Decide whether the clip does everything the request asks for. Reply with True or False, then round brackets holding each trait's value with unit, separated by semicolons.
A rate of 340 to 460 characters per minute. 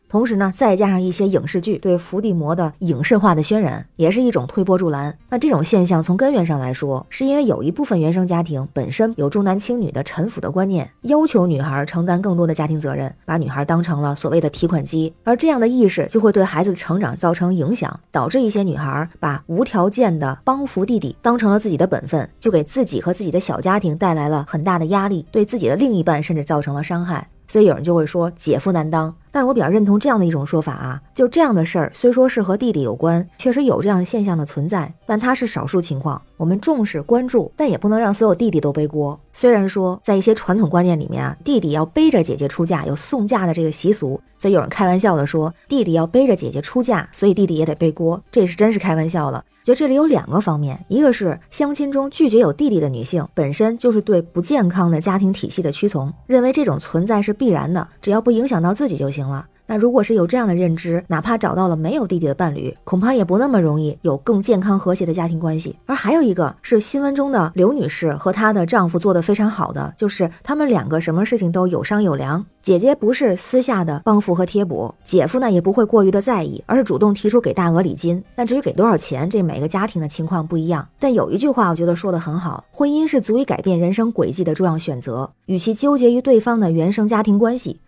True (370 characters per minute)